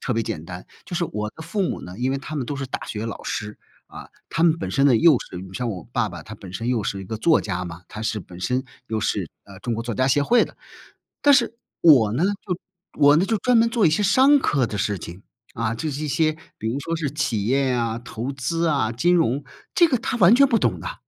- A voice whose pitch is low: Yes, low, 130 Hz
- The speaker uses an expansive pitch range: Yes, wide, 7.3 semitones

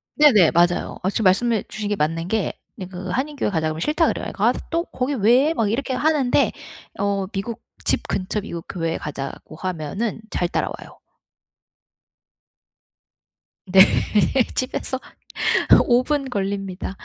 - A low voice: No, high, 200 Hz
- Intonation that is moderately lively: No, wide, 5.7 semitones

